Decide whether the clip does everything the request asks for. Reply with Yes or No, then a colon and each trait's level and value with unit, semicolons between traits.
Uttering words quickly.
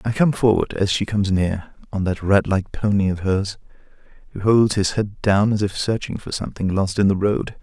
Yes: fast, 220 wpm